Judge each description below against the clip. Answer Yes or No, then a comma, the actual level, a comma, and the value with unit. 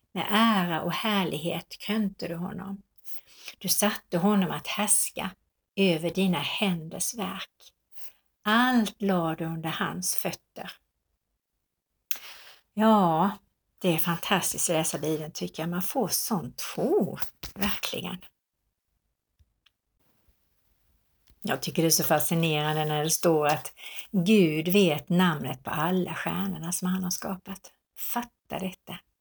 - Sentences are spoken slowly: Yes, slow, 120 wpm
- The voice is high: No, medium, 180 Hz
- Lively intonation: No, average, 3.3 semitones